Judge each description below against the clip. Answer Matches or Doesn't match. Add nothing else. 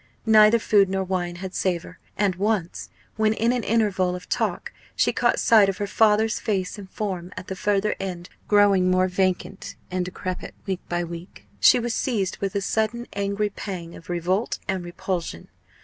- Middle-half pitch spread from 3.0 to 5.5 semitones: Doesn't match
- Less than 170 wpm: Doesn't match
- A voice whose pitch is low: Doesn't match